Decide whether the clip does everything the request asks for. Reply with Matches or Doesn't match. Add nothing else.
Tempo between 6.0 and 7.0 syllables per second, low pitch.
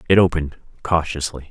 Matches